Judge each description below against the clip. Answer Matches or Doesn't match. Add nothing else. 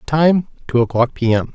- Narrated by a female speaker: Doesn't match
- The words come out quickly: Doesn't match